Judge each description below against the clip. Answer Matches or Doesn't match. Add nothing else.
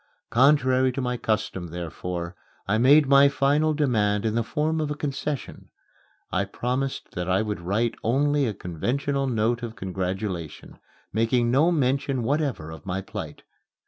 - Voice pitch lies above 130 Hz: Doesn't match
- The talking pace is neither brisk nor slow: Matches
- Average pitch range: Doesn't match